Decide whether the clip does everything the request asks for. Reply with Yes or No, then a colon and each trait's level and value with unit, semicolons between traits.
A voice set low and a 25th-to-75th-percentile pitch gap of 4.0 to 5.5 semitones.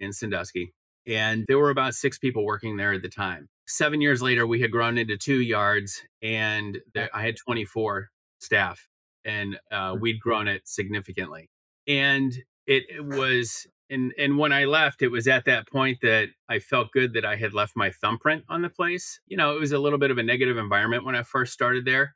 Yes: low, 120 Hz; average, 4.7 semitones